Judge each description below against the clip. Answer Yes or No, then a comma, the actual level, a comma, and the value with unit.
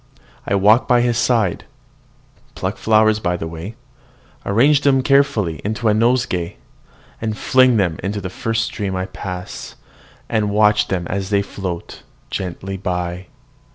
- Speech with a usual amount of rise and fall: Yes, average, 3.6 semitones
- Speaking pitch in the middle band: No, low, 105 Hz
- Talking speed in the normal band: Yes, average, 145 wpm